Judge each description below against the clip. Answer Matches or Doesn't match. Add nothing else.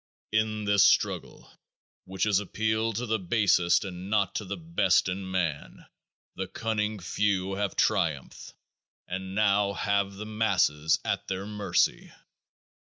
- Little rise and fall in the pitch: Matches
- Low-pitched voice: Matches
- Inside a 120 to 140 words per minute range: Matches